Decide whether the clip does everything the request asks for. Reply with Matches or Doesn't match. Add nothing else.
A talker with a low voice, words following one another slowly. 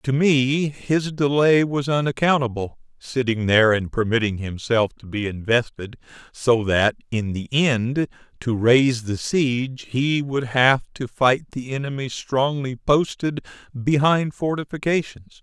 Matches